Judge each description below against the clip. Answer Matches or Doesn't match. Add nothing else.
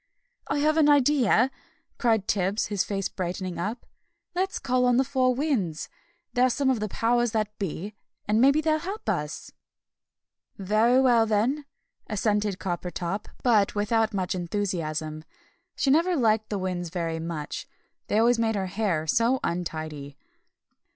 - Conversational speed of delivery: Matches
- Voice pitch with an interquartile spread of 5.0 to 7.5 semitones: Matches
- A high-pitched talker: Matches